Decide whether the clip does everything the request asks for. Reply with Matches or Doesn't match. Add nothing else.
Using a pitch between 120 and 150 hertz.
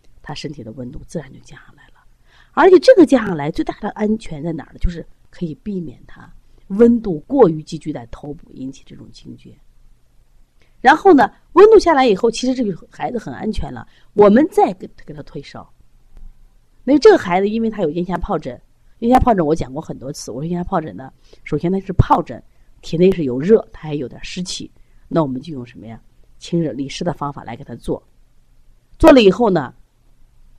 Doesn't match